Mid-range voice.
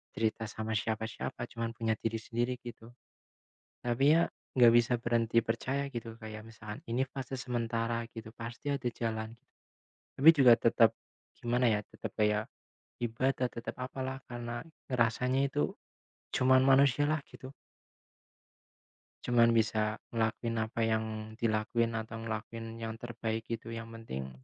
No: low, 115 Hz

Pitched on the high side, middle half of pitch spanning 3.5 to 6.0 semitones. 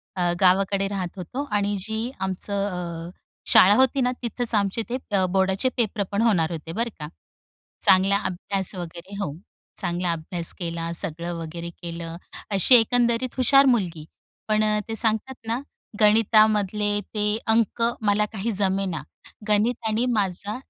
Yes: high, 200 Hz; average, 3.9 semitones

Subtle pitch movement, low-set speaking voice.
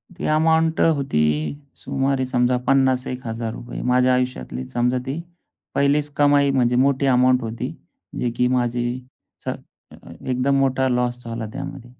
Yes: narrow, 1.9 semitones; low, 130 Hz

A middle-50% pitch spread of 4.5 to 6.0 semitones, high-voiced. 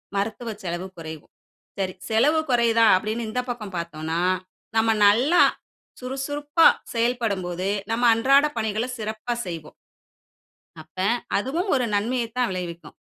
Yes: average, 5.1 semitones; high, 225 Hz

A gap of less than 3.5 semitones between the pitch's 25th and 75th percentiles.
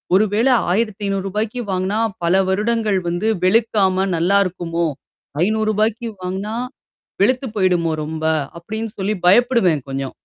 Yes: average, 3.1 semitones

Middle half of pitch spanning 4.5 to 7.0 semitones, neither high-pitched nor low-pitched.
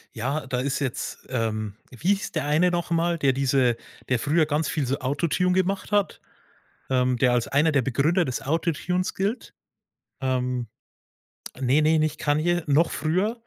Yes: average, 5.0 semitones; medium, 145 Hz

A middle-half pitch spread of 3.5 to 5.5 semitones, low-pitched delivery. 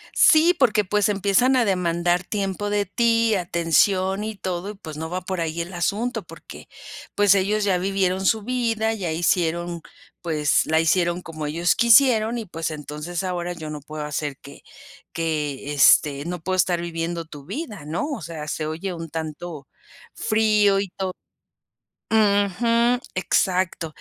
No: average, 4.1 semitones; medium, 180 Hz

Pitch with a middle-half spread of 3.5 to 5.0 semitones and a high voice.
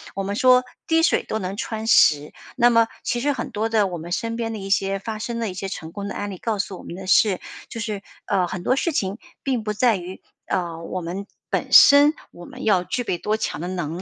Yes: average, 3.8 semitones; high, 200 Hz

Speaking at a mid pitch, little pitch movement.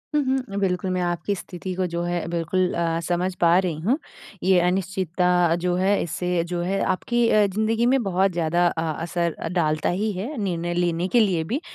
Yes: medium, 180 Hz; narrow, 2.1 semitones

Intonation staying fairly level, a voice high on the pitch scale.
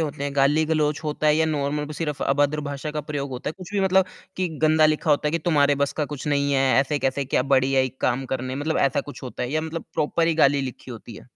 No: narrow, 2.3 semitones; medium, 145 Hz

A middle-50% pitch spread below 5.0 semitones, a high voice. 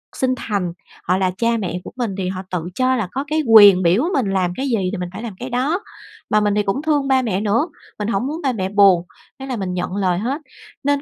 No: wide, 5.6 semitones; high, 210 Hz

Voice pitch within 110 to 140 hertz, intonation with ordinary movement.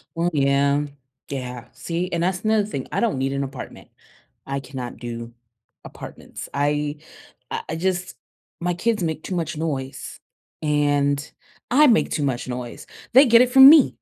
No: medium, 150 Hz; average, 5.0 semitones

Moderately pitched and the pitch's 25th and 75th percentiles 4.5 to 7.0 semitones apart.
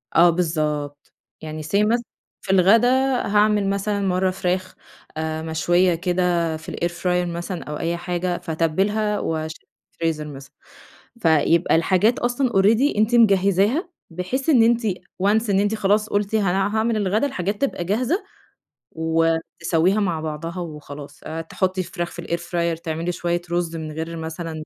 No: medium, 180 Hz; average, 4.1 semitones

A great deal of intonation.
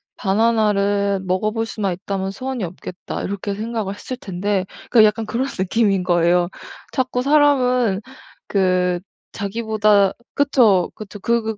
No: average, 3.3 semitones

